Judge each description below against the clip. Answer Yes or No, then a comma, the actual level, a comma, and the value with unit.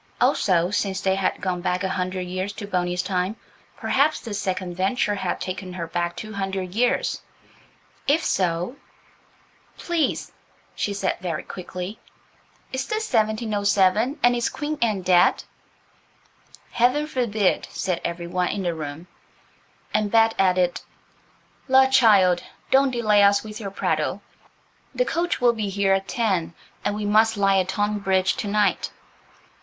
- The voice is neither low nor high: No, high, 200 Hz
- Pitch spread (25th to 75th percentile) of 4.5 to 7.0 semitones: No, average, 3.4 semitones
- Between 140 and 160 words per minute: Yes, average, 145 wpm